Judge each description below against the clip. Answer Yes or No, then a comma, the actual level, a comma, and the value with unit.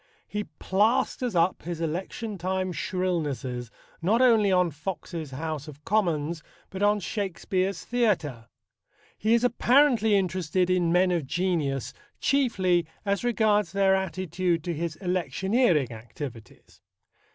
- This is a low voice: No, medium, 185 Hz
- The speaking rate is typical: No, slow, 120 wpm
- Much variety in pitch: No, average, 4.2 semitones